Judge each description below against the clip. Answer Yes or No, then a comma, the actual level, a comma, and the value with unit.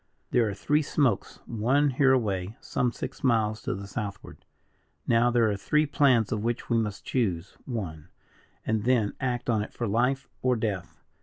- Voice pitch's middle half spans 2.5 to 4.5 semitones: Yes, average, 3.6 semitones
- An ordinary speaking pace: Yes, average, 170 wpm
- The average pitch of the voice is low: Yes, low, 115 Hz